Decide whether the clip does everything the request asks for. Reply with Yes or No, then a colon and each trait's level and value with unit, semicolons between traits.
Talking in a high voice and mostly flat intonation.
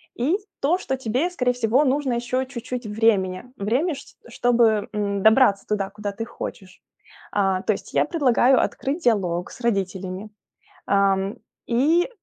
No: high, 230 Hz; average, 4.7 semitones